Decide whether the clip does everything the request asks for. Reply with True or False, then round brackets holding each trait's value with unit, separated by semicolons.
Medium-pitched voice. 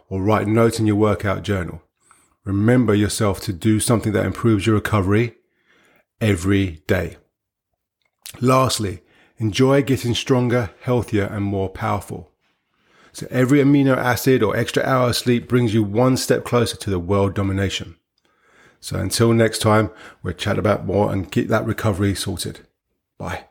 False (110 Hz)